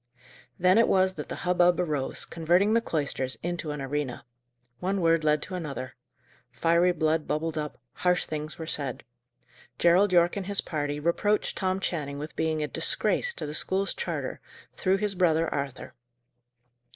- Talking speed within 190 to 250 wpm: No, average, 165 wpm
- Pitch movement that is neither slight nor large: Yes, average, 3.6 semitones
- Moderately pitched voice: Yes, medium, 165 Hz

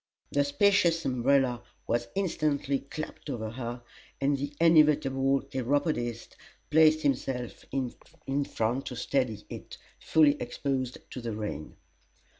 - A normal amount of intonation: Yes, average, 3.1 semitones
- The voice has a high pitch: No, low, 135 Hz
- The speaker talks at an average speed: No, slow, 115 wpm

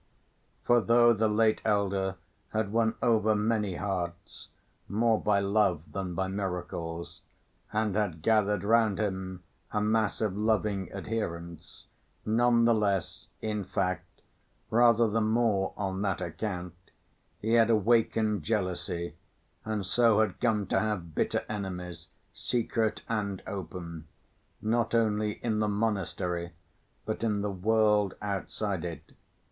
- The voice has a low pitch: Yes, low, 105 Hz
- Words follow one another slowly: Yes, slow, 130 wpm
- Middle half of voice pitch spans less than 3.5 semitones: Yes, average, 2.8 semitones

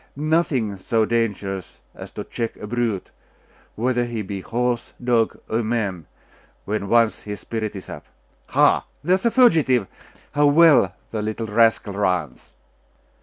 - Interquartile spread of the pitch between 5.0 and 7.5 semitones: No, average, 3.2 semitones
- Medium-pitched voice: No, low, 115 Hz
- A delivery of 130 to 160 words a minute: Yes, average, 145 wpm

